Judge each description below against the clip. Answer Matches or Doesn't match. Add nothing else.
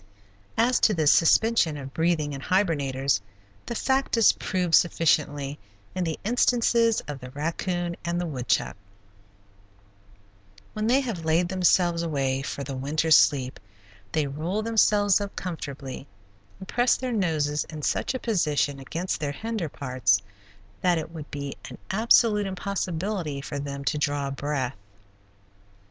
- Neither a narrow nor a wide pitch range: Doesn't match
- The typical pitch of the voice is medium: Matches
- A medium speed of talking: Matches